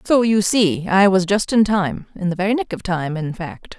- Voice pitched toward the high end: Yes, high, 195 Hz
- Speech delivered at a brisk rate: Yes, fast, 255 wpm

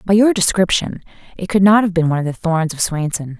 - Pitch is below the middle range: No, medium, 180 Hz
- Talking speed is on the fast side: Yes, fast, 245 wpm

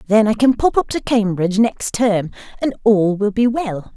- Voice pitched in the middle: No, high, 215 Hz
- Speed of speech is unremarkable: No, fast, 210 wpm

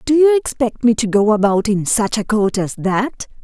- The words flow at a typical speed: No, fast, 225 wpm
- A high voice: Yes, high, 225 Hz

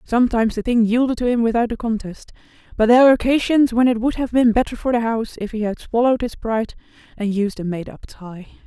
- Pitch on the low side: No, high, 230 Hz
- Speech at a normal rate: No, fast, 235 wpm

